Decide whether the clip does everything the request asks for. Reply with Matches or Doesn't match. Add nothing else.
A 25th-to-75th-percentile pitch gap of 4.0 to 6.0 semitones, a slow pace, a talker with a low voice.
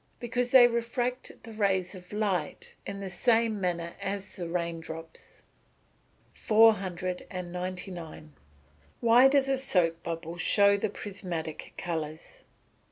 Doesn't match